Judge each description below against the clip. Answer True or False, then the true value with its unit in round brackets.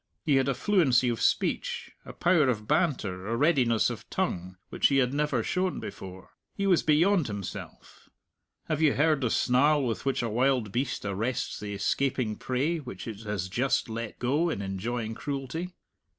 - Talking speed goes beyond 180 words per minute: False (175 wpm)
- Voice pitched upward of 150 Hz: False (130 Hz)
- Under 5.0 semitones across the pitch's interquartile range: False (5.3 semitones)